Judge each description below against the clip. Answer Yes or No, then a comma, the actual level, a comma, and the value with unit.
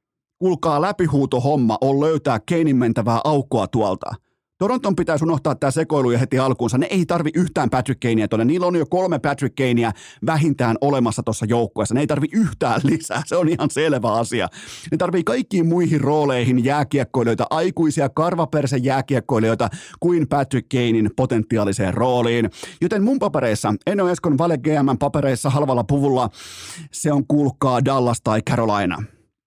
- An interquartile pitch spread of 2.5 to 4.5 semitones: No, average, 4.9 semitones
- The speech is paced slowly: No, average, 150 wpm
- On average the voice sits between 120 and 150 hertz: Yes, medium, 140 Hz